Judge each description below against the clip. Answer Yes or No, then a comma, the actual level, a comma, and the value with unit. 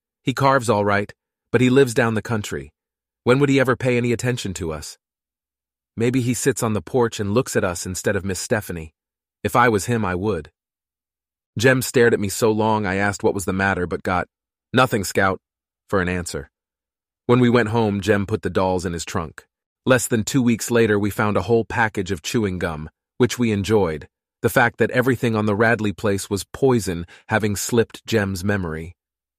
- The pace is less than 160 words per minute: No, average, 200 wpm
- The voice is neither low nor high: No, low, 105 Hz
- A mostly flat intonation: No, average, 4.1 semitones